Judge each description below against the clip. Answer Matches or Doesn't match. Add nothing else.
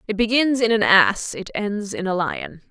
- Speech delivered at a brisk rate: Matches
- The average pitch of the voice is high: Matches